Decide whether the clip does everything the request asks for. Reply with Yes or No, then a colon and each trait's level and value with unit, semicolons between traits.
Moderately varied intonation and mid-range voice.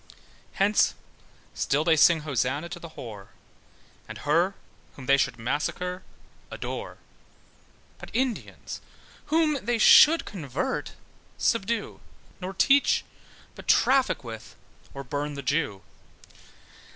No: wide, 7.4 semitones; medium, 165 Hz